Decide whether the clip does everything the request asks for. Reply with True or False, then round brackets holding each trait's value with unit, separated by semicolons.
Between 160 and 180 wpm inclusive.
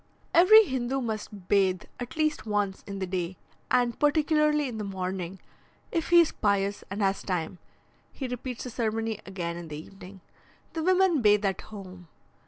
True (170 wpm)